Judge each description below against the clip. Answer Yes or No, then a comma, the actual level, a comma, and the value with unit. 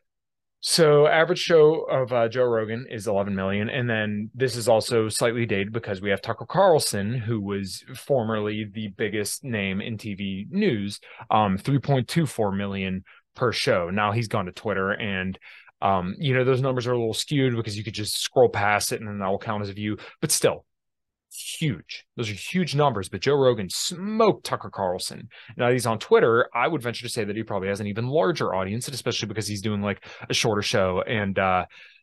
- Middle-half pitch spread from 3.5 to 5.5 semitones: Yes, average, 3.9 semitones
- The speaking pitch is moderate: No, low, 115 Hz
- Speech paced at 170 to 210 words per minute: Yes, average, 200 wpm